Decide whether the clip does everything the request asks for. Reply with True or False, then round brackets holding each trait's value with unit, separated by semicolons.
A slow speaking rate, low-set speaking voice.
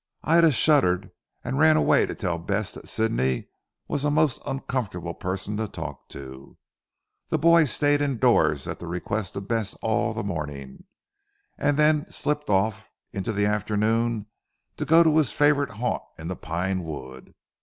False (160 wpm; 110 Hz)